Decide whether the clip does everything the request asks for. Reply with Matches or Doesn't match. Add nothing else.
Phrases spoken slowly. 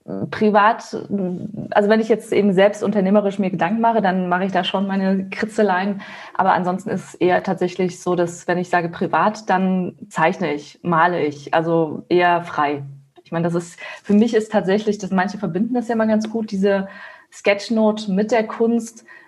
Doesn't match